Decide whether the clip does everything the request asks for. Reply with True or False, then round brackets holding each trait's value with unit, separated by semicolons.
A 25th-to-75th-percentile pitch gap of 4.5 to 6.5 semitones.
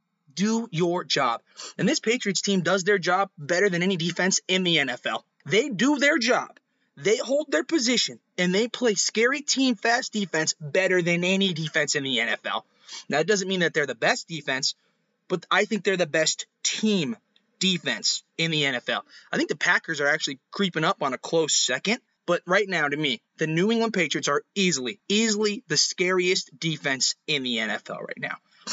True (5.5 semitones)